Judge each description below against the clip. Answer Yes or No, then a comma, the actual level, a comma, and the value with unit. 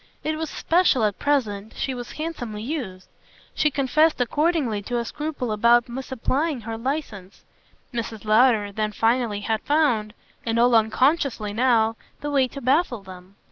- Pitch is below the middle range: No, high, 240 Hz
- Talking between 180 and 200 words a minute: No, average, 150 wpm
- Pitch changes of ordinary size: Yes, average, 4.7 semitones